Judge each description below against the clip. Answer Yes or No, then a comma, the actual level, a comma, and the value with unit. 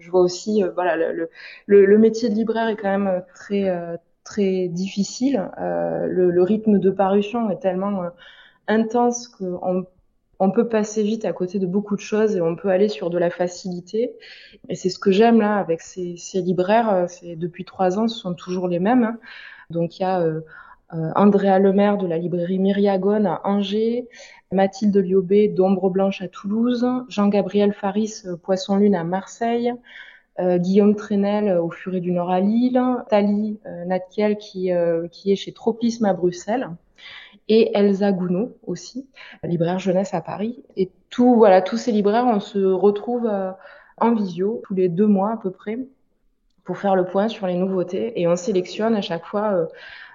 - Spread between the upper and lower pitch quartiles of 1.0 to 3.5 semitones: Yes, average, 3.1 semitones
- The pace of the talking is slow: No, average, 185 wpm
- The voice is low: No, high, 195 Hz